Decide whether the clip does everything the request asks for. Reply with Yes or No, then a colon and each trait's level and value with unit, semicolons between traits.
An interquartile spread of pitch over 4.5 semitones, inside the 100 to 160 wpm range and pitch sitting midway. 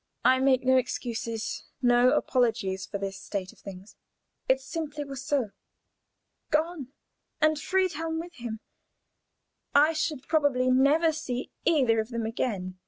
No: average, 5.1 semitones; slow, 135 wpm; very high, 260 Hz